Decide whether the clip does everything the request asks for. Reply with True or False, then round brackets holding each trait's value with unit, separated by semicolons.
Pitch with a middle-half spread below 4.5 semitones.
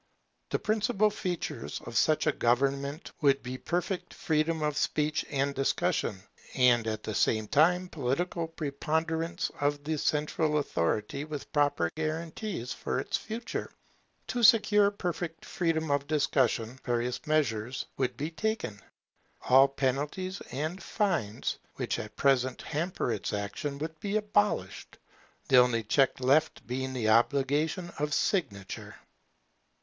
False (4.9 semitones)